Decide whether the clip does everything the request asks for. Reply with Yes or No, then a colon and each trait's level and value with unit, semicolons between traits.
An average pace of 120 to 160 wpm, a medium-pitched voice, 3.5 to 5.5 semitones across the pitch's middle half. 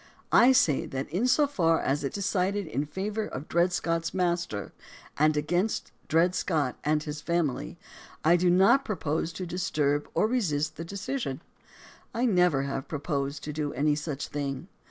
No: average, 170 wpm; medium, 165 Hz; average, 4.1 semitones